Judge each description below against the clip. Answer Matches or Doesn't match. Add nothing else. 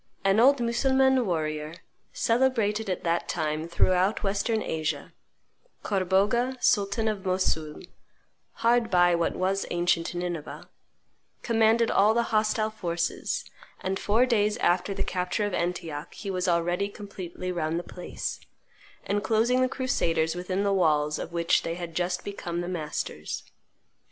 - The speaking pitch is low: Doesn't match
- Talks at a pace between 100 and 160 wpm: Matches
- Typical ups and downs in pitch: Matches